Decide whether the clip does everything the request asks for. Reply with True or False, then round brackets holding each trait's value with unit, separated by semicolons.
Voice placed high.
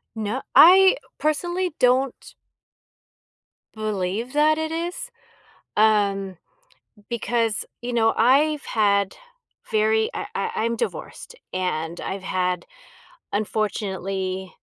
True (220 Hz)